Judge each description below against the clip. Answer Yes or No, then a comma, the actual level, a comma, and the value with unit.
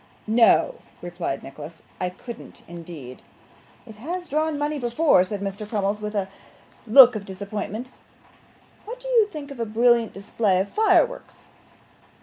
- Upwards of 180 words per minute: No, average, 145 wpm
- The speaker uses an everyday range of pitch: No, wide, 6.8 semitones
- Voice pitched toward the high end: Yes, high, 220 Hz